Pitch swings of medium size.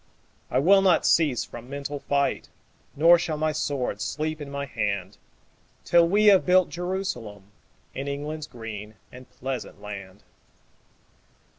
No: wide, 6.1 semitones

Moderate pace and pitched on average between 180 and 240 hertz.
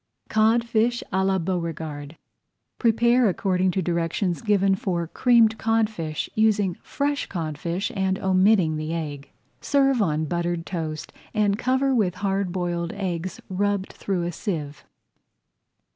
No: slow, 125 wpm; high, 190 Hz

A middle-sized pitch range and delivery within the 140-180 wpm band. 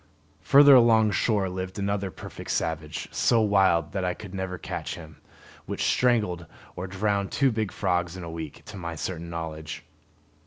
Yes: average, 3.7 semitones; average, 170 wpm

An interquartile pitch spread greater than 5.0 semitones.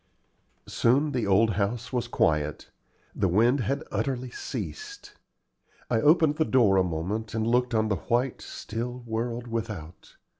No: average, 3.4 semitones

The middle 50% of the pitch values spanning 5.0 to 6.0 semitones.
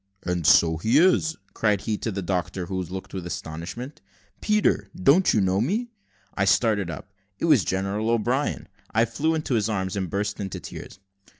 Yes: average, 5.3 semitones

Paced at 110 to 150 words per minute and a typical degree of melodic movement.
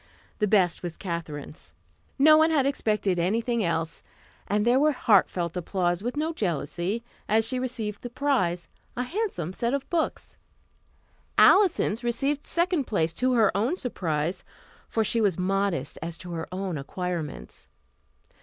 No: average, 145 wpm; wide, 6.6 semitones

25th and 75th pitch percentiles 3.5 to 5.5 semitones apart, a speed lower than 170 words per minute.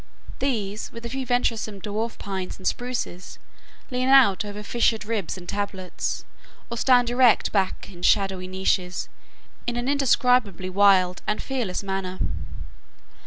Yes: average, 4.3 semitones; slow, 135 wpm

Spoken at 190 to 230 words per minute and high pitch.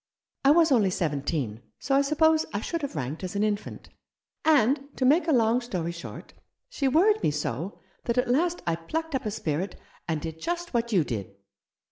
Yes: average, 195 wpm; high, 230 Hz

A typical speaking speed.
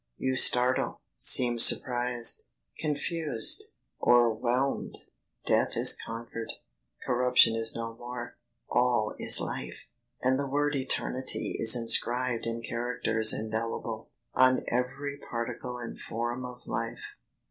No: slow, 110 wpm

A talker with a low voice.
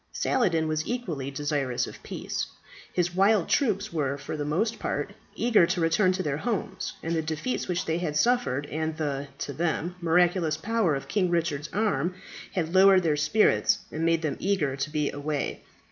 No: medium, 165 Hz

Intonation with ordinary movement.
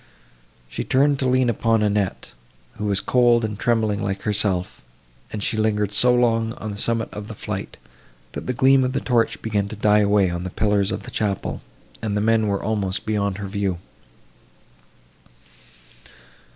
No: narrow, 2.3 semitones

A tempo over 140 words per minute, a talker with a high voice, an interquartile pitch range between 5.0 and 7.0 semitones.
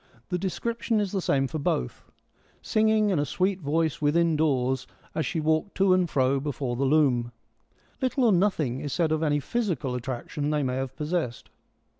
No: average, 195 wpm; medium, 155 Hz; average, 5.3 semitones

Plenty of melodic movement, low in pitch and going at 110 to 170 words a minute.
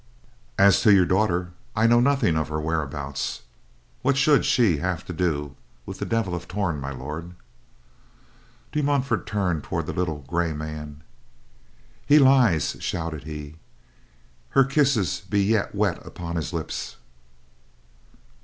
Yes: wide, 5.9 semitones; very low, 90 Hz; average, 140 wpm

